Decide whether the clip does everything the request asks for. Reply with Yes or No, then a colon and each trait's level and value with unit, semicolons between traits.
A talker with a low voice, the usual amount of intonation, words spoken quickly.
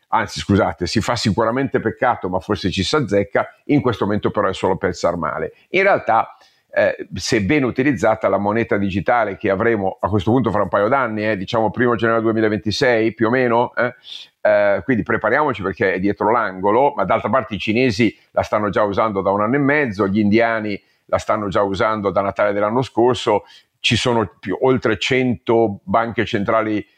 Yes: low, 110 Hz; average, 3.1 semitones; fast, 185 wpm